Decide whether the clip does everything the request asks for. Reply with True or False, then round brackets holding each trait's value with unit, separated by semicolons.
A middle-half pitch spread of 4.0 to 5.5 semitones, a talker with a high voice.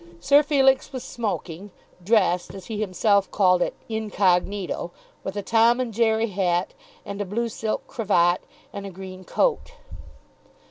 False (3.6 semitones; 205 Hz)